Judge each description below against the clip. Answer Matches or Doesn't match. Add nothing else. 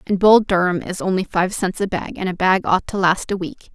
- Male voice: Doesn't match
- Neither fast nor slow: Doesn't match